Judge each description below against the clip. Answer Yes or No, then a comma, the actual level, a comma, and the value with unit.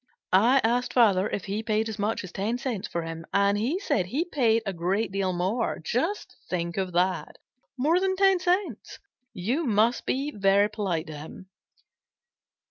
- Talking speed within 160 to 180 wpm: Yes, average, 175 wpm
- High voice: Yes, high, 215 Hz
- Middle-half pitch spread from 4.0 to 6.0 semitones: Yes, average, 5.1 semitones